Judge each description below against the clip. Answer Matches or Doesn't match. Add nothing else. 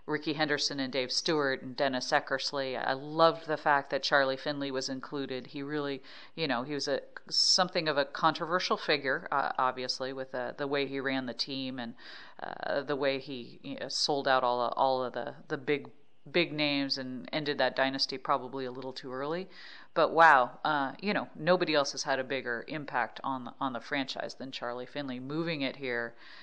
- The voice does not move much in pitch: Matches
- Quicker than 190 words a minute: Matches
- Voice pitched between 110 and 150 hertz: Matches